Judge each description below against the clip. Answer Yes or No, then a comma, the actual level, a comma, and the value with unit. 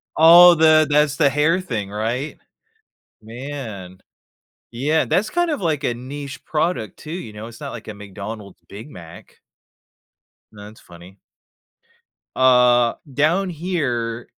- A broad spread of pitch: Yes, wide, 6.3 semitones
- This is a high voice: No, low, 130 Hz